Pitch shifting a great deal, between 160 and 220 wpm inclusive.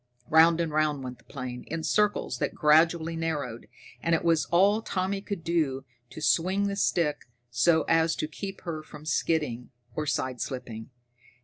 No: average, 2.9 semitones; average, 165 wpm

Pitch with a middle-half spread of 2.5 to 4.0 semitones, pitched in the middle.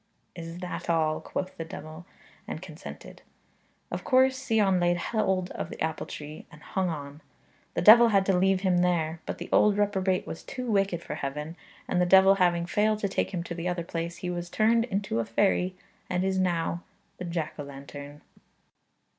Yes: average, 2.9 semitones; medium, 180 Hz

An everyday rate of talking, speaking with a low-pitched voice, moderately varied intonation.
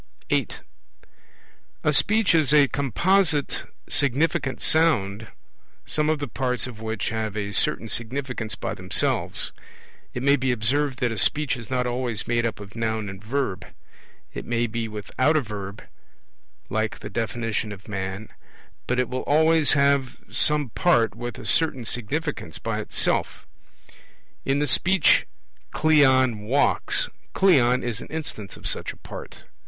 Yes: average, 150 wpm; low, 125 Hz; average, 4.7 semitones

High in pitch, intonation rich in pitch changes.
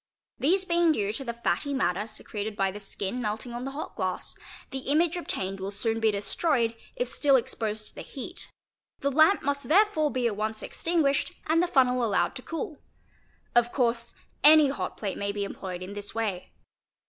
Yes: high, 240 Hz; wide, 5.7 semitones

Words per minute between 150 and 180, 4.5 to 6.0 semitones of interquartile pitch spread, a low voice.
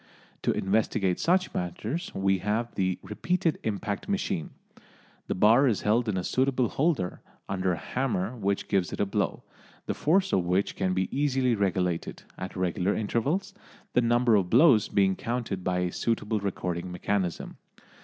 Yes: average, 160 wpm; average, 5.1 semitones; low, 105 Hz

